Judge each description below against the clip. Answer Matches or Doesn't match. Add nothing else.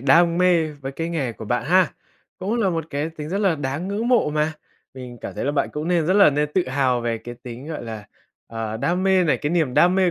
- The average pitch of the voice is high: Doesn't match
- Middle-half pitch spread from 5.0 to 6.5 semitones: Matches